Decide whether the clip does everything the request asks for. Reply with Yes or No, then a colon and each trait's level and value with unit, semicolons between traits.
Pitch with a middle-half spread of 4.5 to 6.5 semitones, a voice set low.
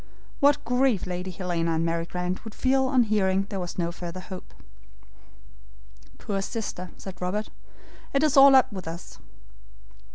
No: average, 5.3 semitones; high, 190 Hz